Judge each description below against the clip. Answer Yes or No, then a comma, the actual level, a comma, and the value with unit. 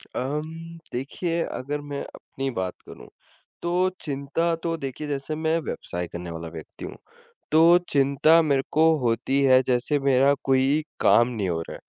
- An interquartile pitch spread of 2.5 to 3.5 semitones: No, average, 3.9 semitones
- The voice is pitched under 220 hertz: Yes, medium, 140 Hz